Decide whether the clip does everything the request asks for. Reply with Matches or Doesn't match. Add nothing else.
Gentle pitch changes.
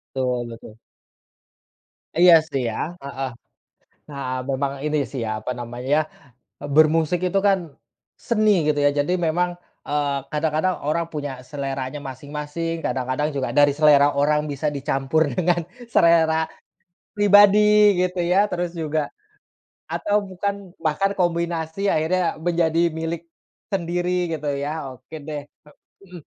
Doesn't match